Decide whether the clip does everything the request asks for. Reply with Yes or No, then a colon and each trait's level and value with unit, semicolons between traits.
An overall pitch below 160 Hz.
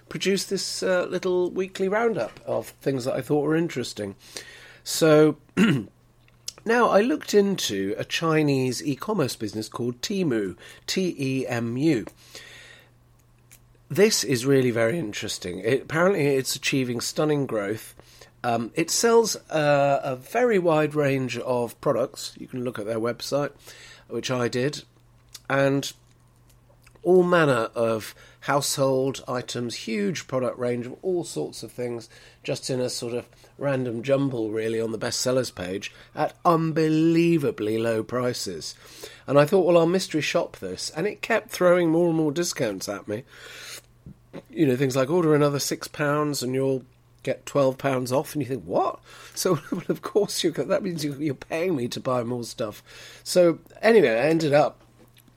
Yes: low, 135 Hz